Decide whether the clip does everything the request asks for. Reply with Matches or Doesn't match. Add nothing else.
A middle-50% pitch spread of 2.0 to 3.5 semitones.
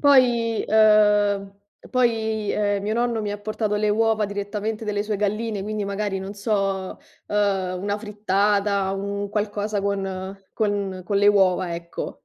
Doesn't match